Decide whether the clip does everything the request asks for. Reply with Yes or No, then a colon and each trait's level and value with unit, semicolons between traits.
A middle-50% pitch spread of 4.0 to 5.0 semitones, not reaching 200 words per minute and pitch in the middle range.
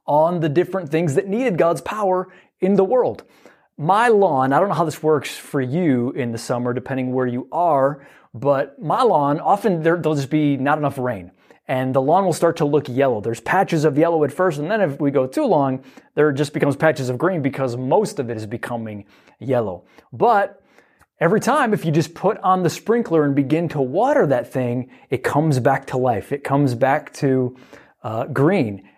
No: average, 4.4 semitones; fast, 205 wpm; medium, 145 Hz